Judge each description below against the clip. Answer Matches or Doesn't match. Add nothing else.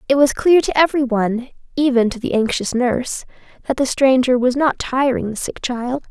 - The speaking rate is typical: Matches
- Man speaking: Doesn't match